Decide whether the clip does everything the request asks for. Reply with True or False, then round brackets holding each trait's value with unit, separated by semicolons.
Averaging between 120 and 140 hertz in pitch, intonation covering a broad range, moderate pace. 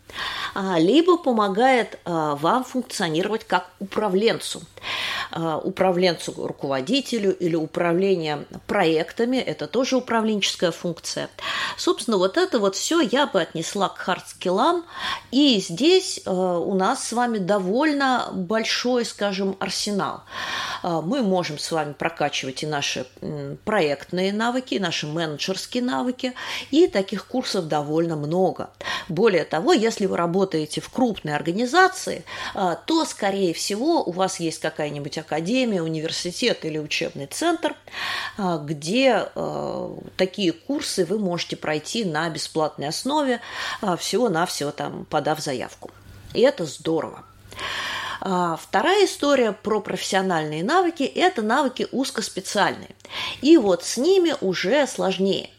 False (190 Hz; 7.3 semitones; 120 wpm)